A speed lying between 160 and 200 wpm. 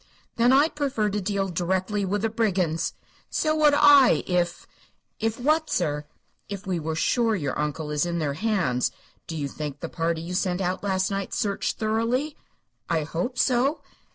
Yes: average, 180 wpm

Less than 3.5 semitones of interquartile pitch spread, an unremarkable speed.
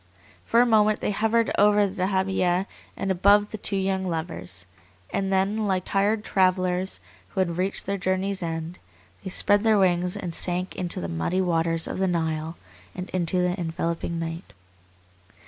Yes: narrow, 2.5 semitones; average, 165 wpm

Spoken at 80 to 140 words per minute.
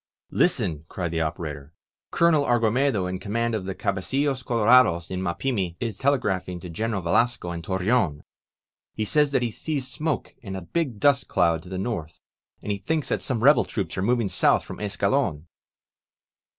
No: average, 165 wpm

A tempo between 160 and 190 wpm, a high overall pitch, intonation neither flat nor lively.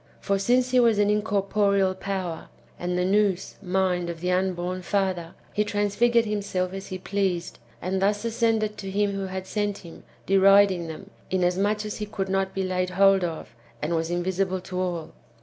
No: average, 180 wpm; high, 195 Hz; narrow, 2.1 semitones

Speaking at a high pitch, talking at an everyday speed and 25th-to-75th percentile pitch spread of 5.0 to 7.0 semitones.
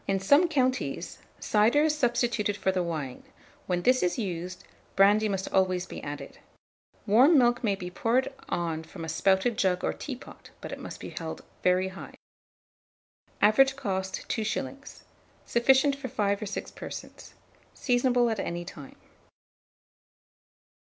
Yes: high, 210 Hz; average, 145 wpm; wide, 5.4 semitones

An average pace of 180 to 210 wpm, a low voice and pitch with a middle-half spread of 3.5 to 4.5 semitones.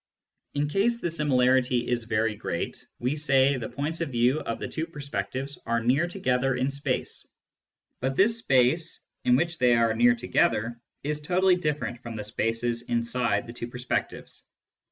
No: average, 165 wpm; low, 130 Hz; average, 4.2 semitones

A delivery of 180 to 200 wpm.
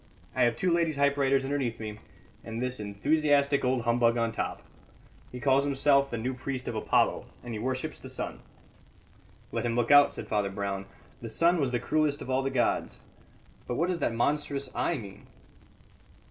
Yes: average, 185 wpm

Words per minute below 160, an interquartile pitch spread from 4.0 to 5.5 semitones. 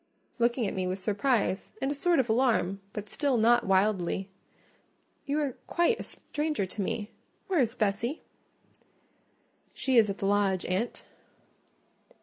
Yes: average, 140 wpm; average, 5.2 semitones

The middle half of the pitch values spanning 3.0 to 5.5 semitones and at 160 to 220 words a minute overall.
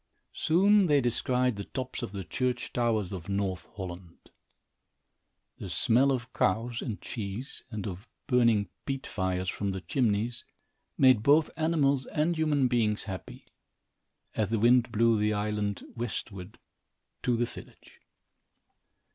No: average, 4.1 semitones; slow, 135 wpm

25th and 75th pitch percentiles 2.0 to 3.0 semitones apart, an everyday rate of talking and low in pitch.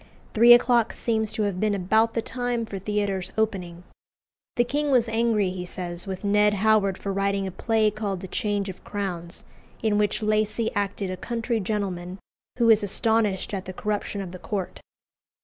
No: narrow, 2.6 semitones; average, 180 wpm; high, 205 Hz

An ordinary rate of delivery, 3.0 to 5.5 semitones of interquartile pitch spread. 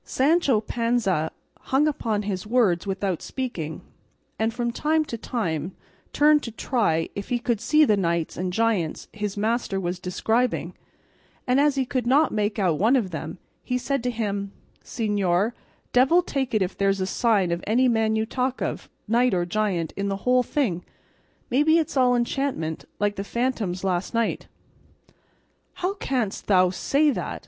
Yes: average, 170 wpm; average, 4.8 semitones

